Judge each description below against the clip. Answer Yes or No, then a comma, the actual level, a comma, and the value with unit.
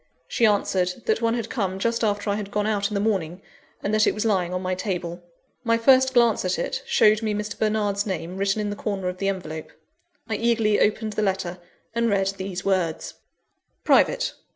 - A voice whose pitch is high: Yes, high, 205 Hz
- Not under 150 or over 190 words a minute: No, fast, 205 wpm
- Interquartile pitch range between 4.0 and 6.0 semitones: No, average, 2.7 semitones